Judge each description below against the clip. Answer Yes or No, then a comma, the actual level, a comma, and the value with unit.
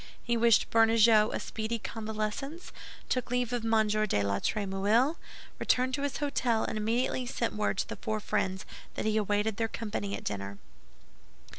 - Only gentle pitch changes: Yes, narrow, 2.2 semitones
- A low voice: No, high, 220 Hz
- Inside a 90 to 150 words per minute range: No, average, 165 wpm